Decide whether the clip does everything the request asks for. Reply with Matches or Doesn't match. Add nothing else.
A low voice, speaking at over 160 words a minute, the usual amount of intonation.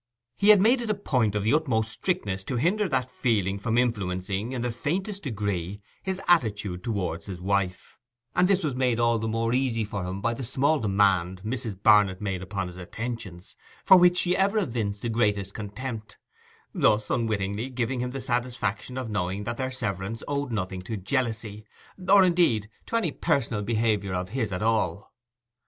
Matches